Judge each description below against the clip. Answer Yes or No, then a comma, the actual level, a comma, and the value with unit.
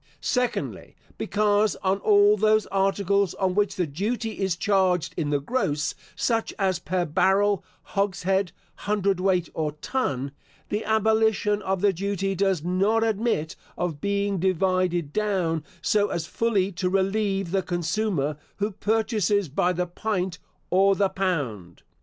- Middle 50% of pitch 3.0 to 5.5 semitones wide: No, narrow, 2.6 semitones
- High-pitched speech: Yes, high, 195 Hz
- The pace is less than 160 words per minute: Yes, average, 140 wpm